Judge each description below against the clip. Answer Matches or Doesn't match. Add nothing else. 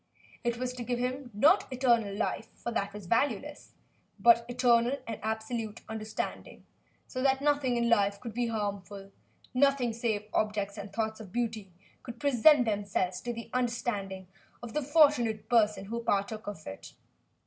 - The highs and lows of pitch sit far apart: Doesn't match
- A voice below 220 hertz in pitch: Doesn't match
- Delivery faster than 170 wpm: Doesn't match